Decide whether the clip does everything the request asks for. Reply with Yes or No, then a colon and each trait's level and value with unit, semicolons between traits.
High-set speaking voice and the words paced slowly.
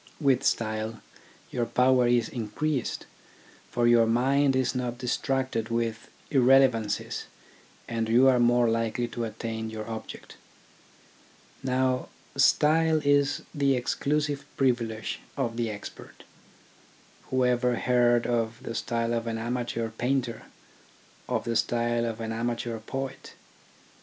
No: low, 120 Hz; slow, 120 wpm